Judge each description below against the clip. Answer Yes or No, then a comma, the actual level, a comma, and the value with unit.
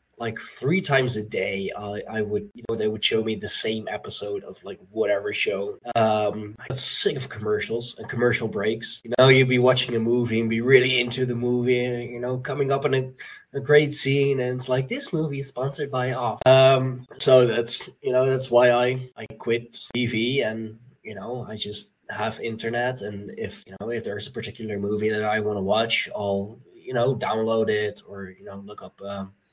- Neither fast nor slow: No, fast, 210 wpm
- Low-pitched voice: Yes, low, 120 Hz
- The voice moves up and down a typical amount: Yes, average, 3.1 semitones